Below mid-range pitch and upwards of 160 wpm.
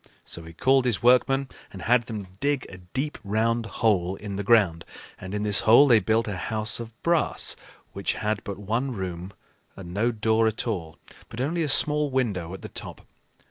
Yes: low, 110 Hz; average, 195 wpm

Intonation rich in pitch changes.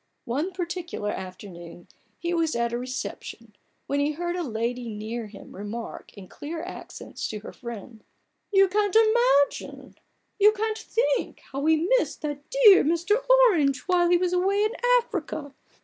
Yes: wide, 8.2 semitones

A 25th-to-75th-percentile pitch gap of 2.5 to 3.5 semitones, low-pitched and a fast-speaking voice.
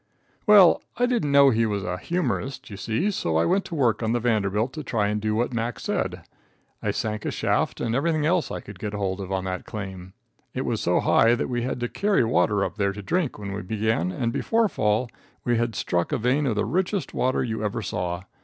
No: average, 4.9 semitones; low, 115 Hz; fast, 235 wpm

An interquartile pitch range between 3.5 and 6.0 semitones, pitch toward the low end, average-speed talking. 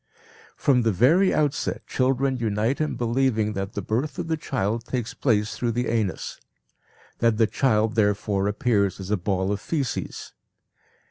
Yes: average, 4.1 semitones; low, 115 Hz; average, 155 wpm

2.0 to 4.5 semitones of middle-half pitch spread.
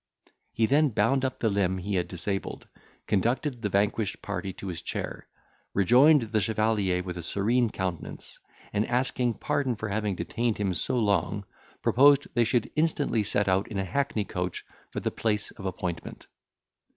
Yes: average, 4.0 semitones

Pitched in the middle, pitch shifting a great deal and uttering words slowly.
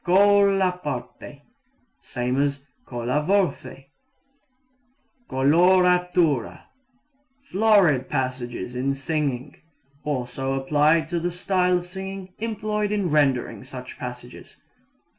Yes: medium, 155 Hz; wide, 6.0 semitones; slow, 90 wpm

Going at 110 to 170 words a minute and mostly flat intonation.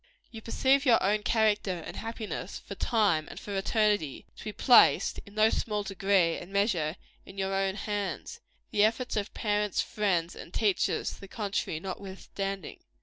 Yes: average, 165 wpm; narrow, 2.0 semitones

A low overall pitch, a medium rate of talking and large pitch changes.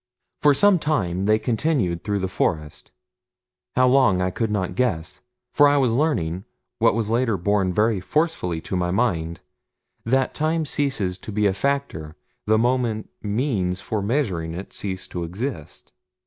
Yes: low, 105 Hz; average, 160 wpm; wide, 6.2 semitones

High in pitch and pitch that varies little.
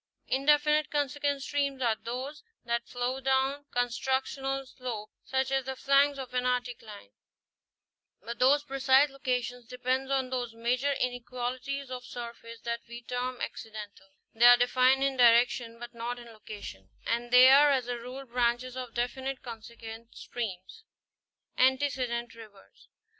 Yes: very high, 250 Hz; narrow, 2.2 semitones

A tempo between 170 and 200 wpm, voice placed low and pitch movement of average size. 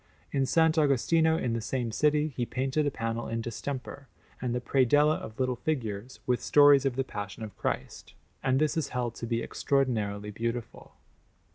Yes: average, 175 wpm; low, 130 Hz; average, 3.7 semitones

